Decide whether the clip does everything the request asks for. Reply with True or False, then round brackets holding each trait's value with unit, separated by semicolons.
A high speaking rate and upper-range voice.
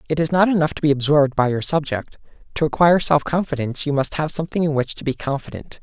False (225 wpm; 150 Hz)